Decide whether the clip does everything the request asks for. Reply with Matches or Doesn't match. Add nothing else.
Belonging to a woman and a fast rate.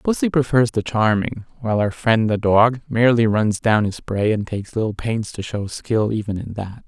Doesn't match